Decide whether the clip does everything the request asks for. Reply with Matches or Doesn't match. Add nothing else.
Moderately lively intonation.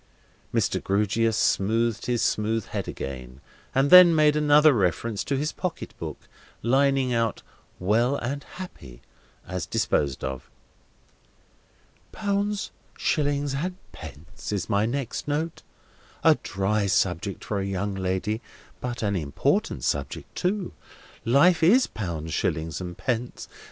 Doesn't match